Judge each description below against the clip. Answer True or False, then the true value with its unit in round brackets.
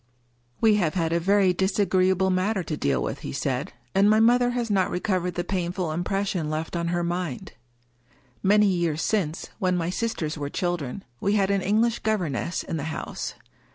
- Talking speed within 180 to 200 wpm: True (185 wpm)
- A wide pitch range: False (3.4 semitones)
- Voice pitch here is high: False (180 Hz)